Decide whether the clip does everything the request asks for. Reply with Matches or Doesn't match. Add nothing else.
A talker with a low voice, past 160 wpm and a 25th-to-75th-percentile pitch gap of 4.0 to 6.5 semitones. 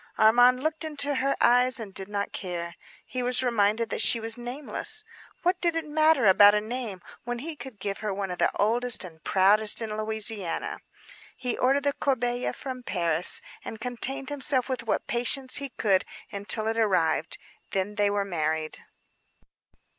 Doesn't match